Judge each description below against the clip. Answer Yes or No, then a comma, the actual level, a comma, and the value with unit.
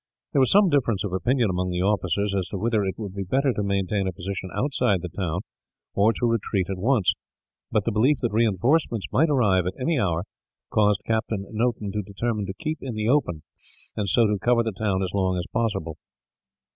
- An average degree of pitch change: Yes, average, 3.9 semitones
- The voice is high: No, low, 105 Hz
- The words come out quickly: Yes, fast, 210 wpm